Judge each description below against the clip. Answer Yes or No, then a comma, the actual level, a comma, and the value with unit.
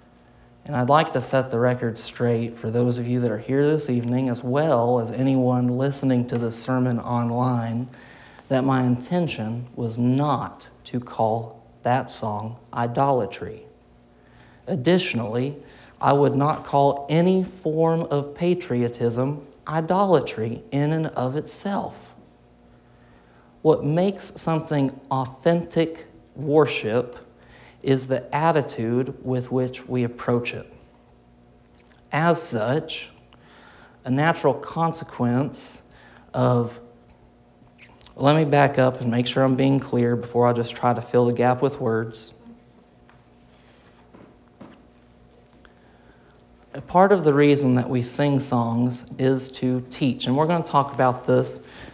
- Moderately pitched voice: No, low, 125 Hz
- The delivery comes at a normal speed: No, slow, 125 wpm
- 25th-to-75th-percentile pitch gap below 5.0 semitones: Yes, average, 3.6 semitones